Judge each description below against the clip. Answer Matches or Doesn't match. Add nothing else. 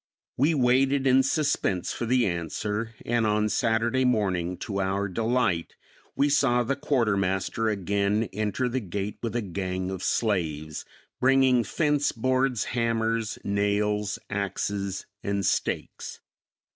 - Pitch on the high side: Doesn't match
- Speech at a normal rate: Doesn't match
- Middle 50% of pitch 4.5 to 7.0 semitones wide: Doesn't match